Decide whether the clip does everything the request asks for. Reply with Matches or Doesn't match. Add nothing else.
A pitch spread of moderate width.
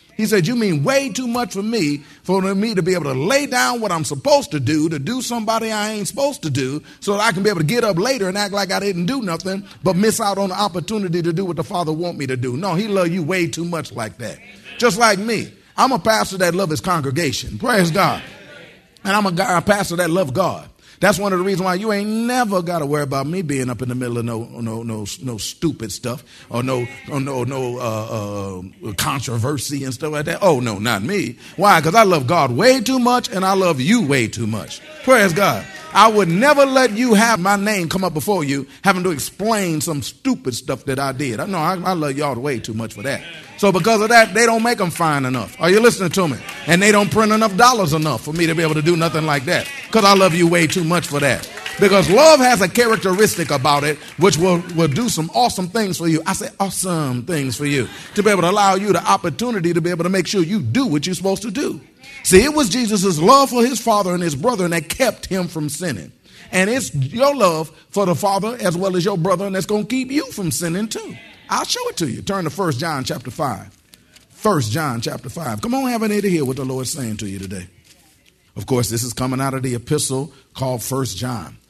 Doesn't match